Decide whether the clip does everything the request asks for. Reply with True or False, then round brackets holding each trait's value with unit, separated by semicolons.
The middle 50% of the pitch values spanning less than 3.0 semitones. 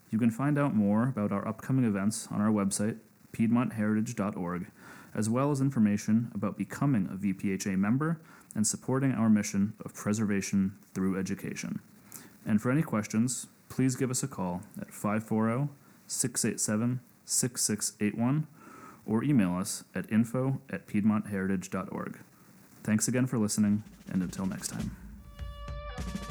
False (3.8 semitones)